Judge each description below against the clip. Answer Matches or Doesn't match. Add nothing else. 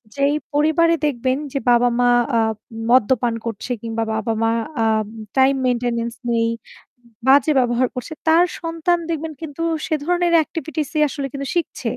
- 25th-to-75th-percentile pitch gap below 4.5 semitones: Doesn't match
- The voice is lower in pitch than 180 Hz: Doesn't match